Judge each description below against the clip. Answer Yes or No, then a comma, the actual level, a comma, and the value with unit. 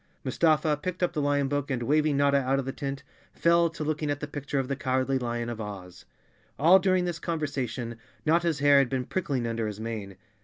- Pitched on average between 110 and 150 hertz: Yes, medium, 140 Hz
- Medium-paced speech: No, fast, 225 wpm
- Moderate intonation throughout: Yes, average, 3.6 semitones